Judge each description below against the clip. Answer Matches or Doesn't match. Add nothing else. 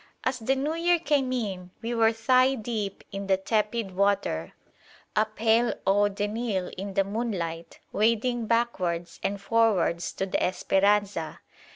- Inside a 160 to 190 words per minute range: Doesn't match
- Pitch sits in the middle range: Doesn't match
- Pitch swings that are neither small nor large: Matches